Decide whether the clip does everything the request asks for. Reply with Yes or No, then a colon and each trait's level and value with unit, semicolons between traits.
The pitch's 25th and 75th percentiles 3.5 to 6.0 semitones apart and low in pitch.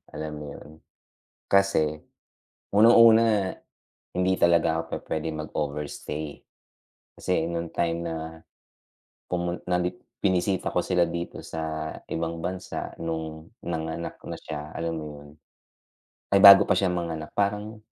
No: average, 3.0 semitones; very low, 85 Hz